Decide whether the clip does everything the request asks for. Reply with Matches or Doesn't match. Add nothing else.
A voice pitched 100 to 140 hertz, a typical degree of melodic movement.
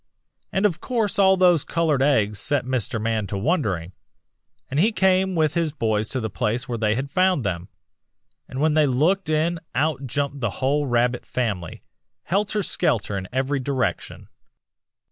Doesn't match